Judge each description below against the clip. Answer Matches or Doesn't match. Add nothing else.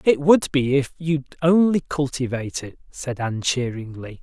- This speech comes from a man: Matches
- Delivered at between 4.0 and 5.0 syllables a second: Matches